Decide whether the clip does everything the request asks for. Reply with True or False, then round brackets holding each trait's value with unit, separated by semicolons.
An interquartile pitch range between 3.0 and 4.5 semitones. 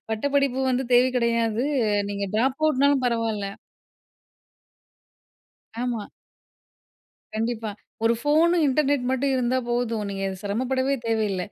True (3.3 semitones)